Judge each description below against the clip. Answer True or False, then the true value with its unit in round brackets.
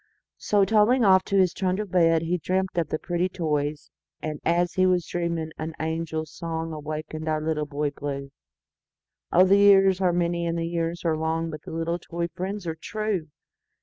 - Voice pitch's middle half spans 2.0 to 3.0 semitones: True (2.7 semitones)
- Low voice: False (170 Hz)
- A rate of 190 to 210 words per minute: False (160 wpm)